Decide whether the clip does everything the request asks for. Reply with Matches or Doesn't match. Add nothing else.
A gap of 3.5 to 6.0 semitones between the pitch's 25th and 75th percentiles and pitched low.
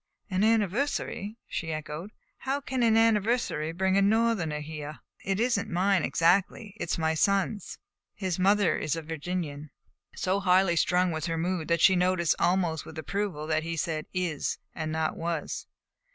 Doesn't match